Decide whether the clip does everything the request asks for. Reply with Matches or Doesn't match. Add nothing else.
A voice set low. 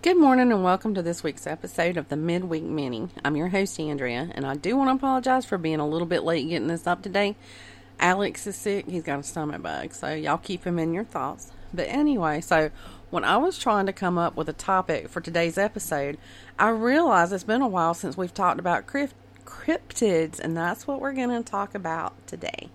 Doesn't match